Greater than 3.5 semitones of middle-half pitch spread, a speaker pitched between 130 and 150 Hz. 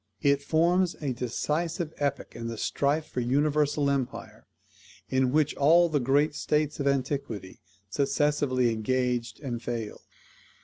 No: average, 3.2 semitones; medium, 140 Hz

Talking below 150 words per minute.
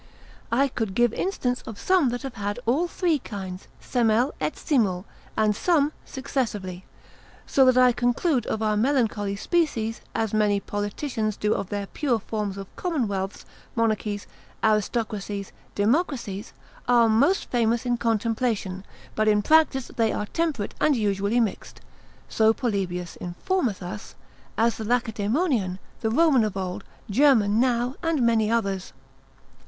Yes: average, 140 wpm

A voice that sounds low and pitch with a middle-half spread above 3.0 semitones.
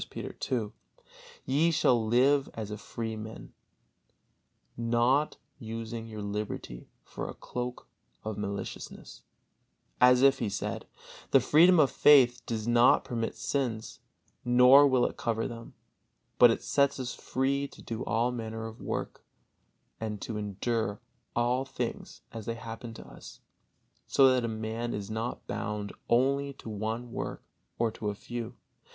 No: low, 115 Hz; narrow, 2.5 semitones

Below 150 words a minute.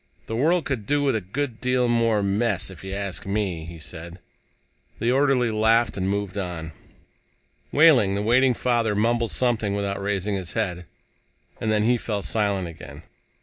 No: average, 170 wpm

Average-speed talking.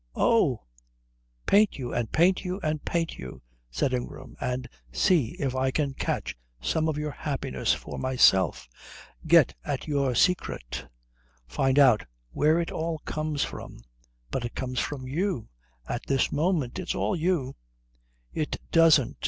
Yes: average, 155 wpm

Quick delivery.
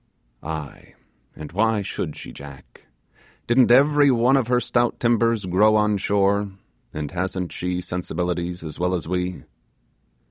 No: average, 140 wpm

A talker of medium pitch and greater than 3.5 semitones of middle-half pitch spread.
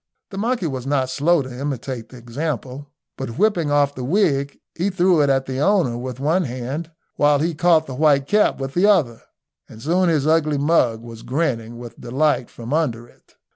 Yes: medium, 145 Hz; average, 4.5 semitones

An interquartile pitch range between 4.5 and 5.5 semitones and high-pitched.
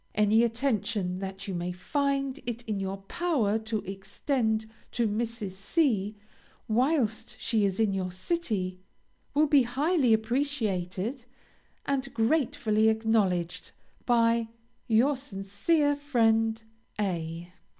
Yes: average, 5.0 semitones; high, 220 Hz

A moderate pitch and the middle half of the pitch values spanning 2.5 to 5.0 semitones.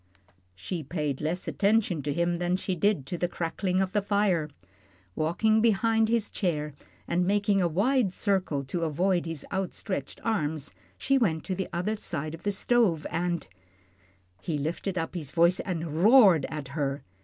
Yes: medium, 175 Hz; average, 4.1 semitones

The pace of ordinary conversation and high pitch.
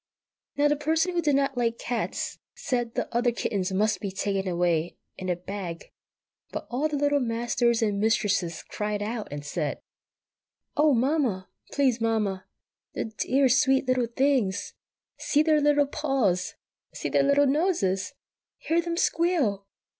Yes: average, 155 wpm; high, 240 Hz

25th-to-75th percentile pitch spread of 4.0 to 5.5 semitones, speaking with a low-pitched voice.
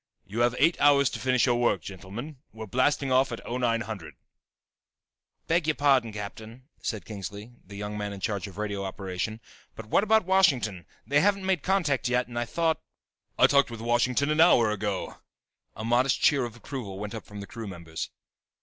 Yes: average, 5.2 semitones; low, 120 Hz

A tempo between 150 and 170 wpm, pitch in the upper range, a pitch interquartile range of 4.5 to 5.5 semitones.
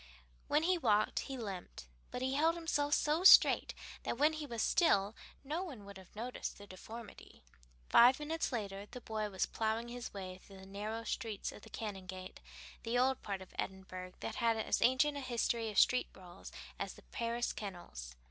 No: average, 185 wpm; high, 225 Hz; average, 5.0 semitones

